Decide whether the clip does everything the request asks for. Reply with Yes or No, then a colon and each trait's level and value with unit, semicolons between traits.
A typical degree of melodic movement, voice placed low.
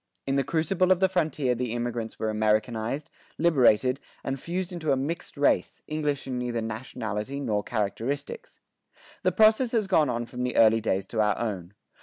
No: wide, 5.8 semitones; low, 125 Hz